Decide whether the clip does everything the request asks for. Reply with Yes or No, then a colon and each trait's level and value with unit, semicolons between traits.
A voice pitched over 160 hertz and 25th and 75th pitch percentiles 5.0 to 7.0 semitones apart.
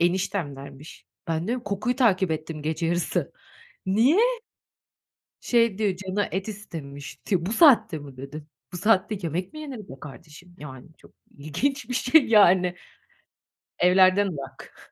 Yes: medium, 185 Hz; wide, 5.5 semitones